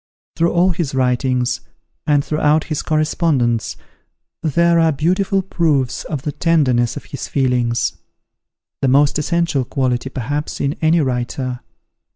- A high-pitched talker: No, medium, 145 Hz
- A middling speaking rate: No, slow, 130 wpm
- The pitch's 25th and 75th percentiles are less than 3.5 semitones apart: No, average, 4.3 semitones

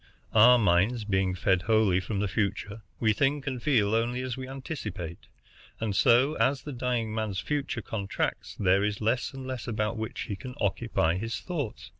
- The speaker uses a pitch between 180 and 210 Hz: No, low, 110 Hz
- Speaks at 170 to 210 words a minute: Yes, average, 180 wpm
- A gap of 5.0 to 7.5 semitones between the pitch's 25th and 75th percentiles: No, average, 4.0 semitones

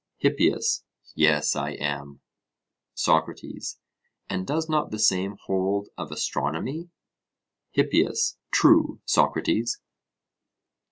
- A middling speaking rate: No, slow, 90 wpm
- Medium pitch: No, very low, 95 Hz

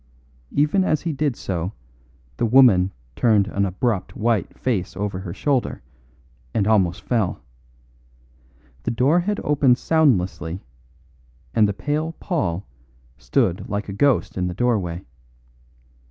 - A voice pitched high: No, low, 110 Hz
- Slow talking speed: Yes, slow, 125 wpm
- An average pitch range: No, wide, 7.0 semitones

